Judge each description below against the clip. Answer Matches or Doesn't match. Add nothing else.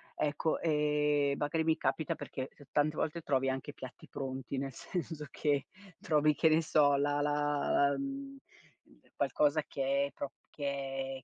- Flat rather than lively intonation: Matches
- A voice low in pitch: Doesn't match